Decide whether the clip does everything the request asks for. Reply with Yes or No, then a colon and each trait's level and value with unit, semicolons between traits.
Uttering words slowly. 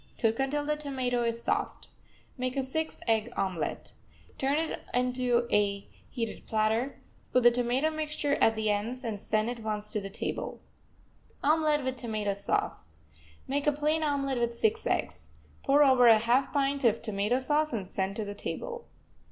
No: average, 170 wpm